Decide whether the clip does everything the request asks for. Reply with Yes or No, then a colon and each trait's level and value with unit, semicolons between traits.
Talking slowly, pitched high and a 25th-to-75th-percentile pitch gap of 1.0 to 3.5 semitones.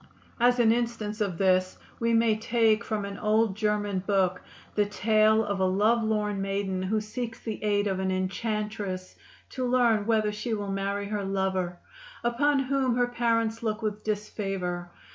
No: average, 160 wpm; high, 210 Hz; narrow, 2.6 semitones